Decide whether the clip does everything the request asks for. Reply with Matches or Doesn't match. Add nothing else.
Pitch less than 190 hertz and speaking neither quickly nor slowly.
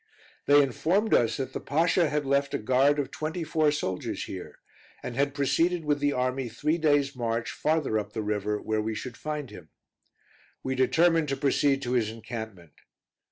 Matches